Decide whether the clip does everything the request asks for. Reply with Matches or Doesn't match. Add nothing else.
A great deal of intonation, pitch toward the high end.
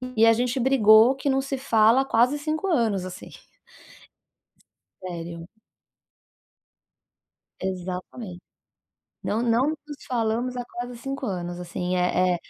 Matches